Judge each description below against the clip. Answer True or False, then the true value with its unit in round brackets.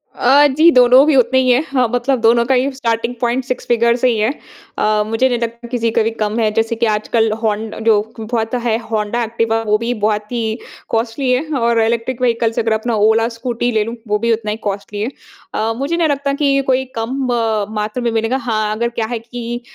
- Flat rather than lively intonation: True (2.1 semitones)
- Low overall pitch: False (235 Hz)